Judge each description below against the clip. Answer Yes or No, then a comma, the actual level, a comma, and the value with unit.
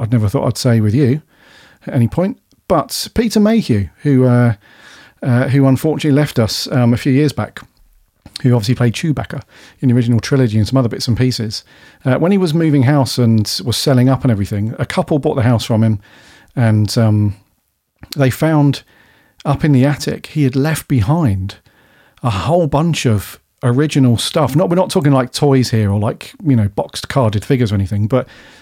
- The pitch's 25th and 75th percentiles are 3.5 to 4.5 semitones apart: Yes, average, 4.2 semitones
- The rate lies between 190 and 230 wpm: Yes, average, 195 wpm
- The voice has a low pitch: Yes, low, 130 Hz